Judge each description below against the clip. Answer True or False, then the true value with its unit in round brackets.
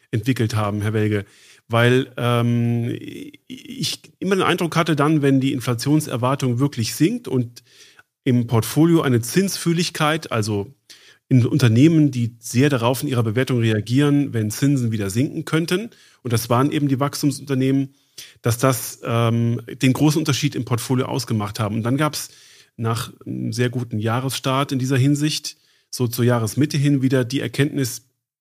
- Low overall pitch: True (130 Hz)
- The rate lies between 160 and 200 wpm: False (150 wpm)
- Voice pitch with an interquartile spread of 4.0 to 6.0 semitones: False (3.6 semitones)